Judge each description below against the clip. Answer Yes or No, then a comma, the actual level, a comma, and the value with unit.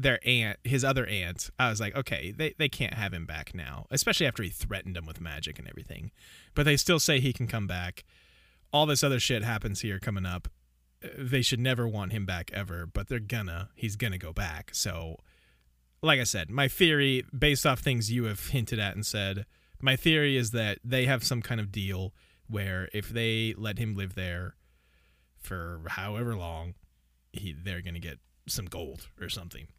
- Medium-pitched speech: No, low, 105 Hz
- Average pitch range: No, wide, 6.2 semitones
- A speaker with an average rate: Yes, average, 195 wpm